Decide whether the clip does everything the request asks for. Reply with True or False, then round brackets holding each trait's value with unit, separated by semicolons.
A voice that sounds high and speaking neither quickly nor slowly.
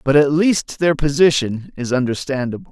False (140 Hz; 155 wpm)